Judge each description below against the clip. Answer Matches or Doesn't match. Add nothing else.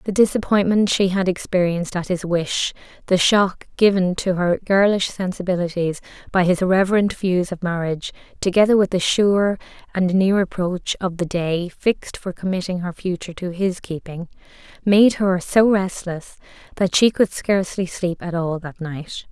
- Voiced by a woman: Matches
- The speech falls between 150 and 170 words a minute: Matches